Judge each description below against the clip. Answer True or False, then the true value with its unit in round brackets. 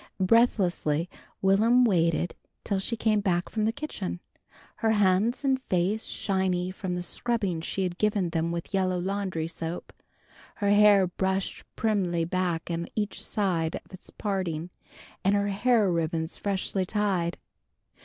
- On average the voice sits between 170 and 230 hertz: True (190 Hz)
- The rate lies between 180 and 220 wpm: False (145 wpm)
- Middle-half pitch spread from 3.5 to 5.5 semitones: False (3.1 semitones)